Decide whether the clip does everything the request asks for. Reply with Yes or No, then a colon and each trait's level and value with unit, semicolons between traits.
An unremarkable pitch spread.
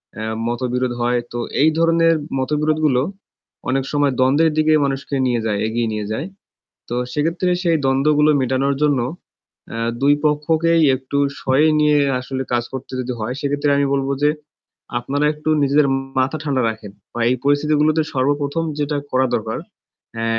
Yes: average, 3.0 semitones